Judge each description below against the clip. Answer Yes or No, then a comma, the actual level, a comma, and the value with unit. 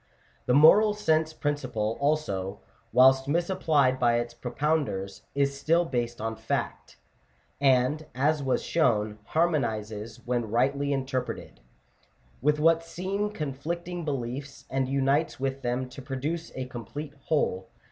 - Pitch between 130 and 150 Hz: Yes, low, 135 Hz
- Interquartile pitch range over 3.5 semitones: Yes, average, 4.2 semitones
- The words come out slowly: Yes, slow, 125 wpm